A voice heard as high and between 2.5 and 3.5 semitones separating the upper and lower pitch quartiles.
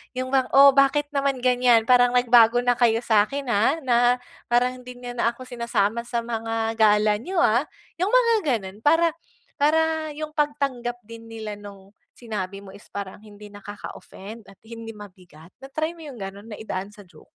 No: high, 235 Hz; average, 4.2 semitones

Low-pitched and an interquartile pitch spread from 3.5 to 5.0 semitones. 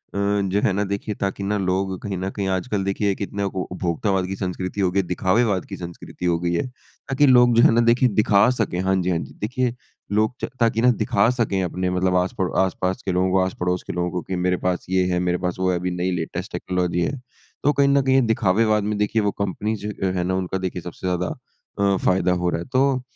No: very low, 95 Hz; average, 2.7 semitones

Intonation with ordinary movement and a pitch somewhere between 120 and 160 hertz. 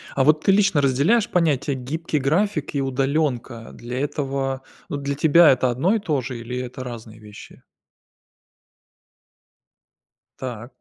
Yes: average, 3.6 semitones; low, 135 Hz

